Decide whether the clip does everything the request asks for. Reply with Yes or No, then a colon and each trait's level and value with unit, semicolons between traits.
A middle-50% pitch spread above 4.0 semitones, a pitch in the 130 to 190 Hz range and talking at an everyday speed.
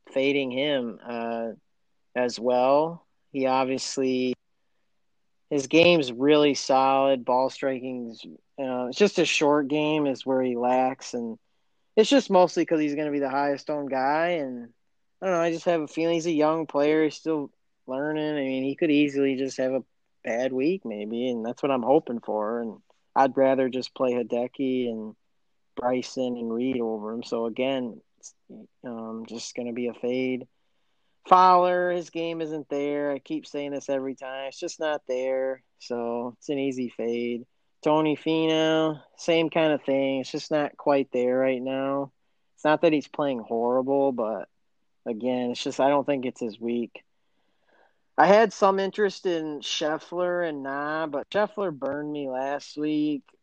No: average, 3.5 semitones; low, 135 Hz; average, 170 wpm